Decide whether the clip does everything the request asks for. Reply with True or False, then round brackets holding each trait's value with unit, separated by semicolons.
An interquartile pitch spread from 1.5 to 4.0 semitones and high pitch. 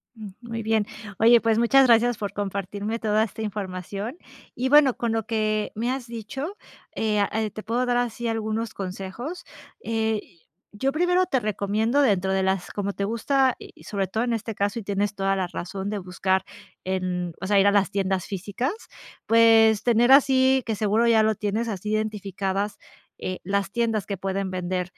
True (2.9 semitones; 215 Hz)